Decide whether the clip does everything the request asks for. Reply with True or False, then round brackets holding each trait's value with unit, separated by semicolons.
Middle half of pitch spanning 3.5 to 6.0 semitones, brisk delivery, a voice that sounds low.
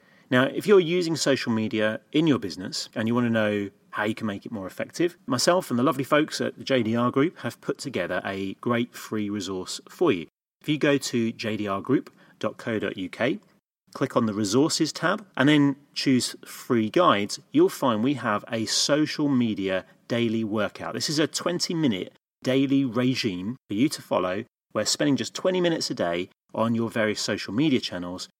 False (5.2 semitones; 180 wpm; 120 Hz)